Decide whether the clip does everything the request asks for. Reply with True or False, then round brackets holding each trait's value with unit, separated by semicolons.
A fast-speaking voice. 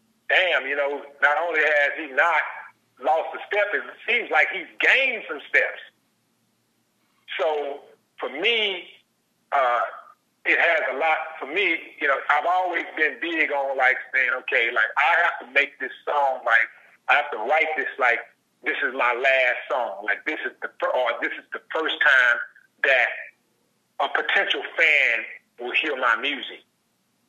False (165 wpm)